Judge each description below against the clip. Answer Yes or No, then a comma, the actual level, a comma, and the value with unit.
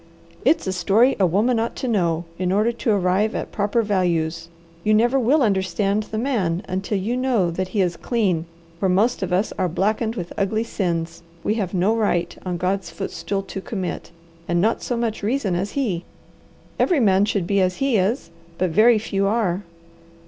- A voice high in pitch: Yes, high, 200 Hz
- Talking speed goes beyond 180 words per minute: Yes, average, 190 wpm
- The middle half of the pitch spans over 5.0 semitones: No, average, 3.6 semitones